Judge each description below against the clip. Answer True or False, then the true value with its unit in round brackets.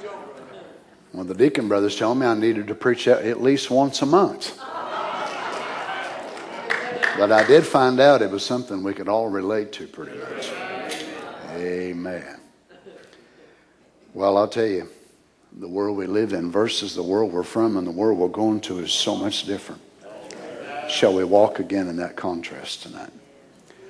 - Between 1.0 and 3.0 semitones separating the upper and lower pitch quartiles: False (4.3 semitones)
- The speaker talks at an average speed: True (160 wpm)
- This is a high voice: False (105 Hz)